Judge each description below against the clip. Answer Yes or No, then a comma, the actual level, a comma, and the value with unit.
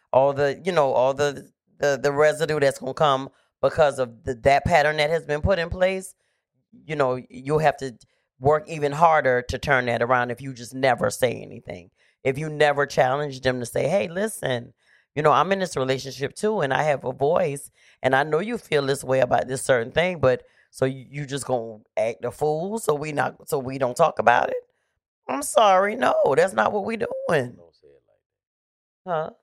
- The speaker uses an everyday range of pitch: Yes, average, 3.4 semitones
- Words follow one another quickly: Yes, fast, 210 wpm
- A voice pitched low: No, medium, 145 Hz